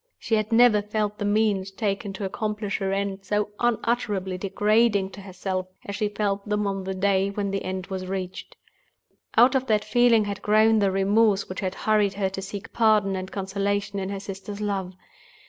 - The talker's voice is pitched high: Yes, high, 200 Hz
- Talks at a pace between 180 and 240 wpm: Yes, average, 190 wpm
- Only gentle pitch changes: Yes, narrow, 1.6 semitones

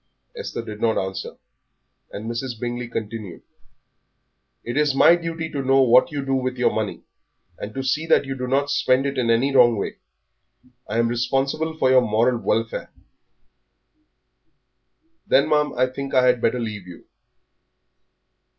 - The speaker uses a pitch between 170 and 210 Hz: No, low, 125 Hz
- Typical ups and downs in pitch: Yes, average, 3.0 semitones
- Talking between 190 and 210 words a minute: No, average, 160 wpm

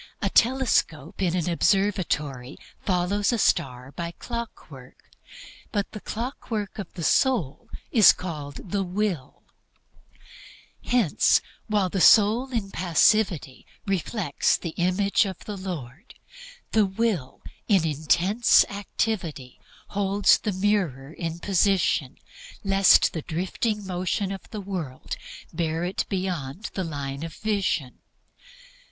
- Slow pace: Yes, slow, 115 wpm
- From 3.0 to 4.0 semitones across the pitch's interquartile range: No, average, 4.5 semitones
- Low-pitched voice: No, medium, 185 Hz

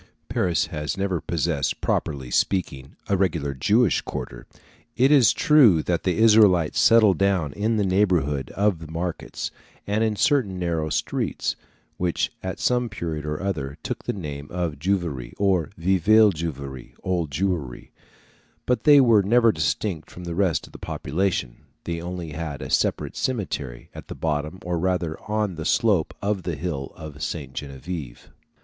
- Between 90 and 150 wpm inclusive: No, average, 160 wpm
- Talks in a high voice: No, very low, 90 Hz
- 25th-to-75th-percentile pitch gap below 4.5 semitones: No, average, 4.8 semitones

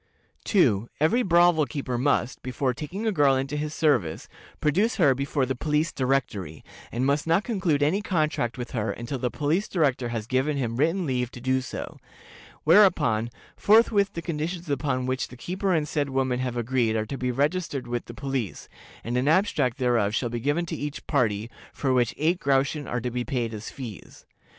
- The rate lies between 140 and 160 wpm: No, average, 190 wpm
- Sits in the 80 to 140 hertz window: Yes, low, 135 Hz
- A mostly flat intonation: No, average, 4.3 semitones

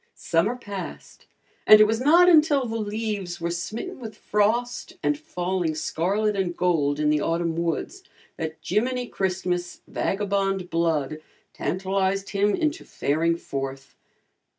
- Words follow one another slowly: Yes, slow, 130 wpm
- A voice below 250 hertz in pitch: Yes, high, 190 Hz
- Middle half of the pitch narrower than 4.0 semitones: No, average, 4.5 semitones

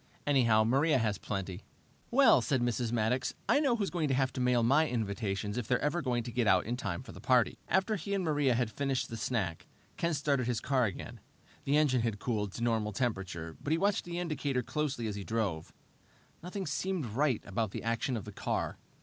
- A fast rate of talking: Yes, fast, 210 wpm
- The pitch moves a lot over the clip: No, average, 5.0 semitones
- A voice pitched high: No, low, 125 Hz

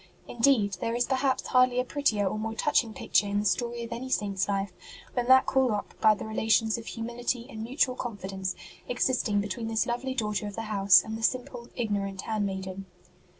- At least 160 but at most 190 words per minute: No, fast, 205 wpm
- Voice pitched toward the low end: No, high, 225 Hz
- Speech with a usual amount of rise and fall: Yes, average, 3.2 semitones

